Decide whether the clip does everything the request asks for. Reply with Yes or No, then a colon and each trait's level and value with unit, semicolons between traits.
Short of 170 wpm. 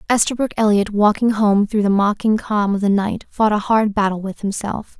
No: fast, 205 wpm